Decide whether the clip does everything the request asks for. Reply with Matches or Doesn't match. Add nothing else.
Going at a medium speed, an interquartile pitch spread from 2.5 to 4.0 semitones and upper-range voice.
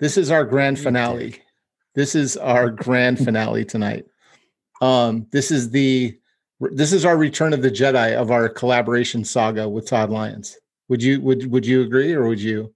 Doesn't match